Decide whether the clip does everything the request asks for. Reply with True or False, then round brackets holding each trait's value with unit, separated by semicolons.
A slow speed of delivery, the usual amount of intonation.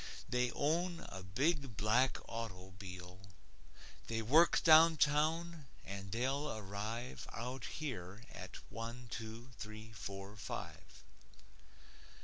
False (100 wpm; 6.3 semitones)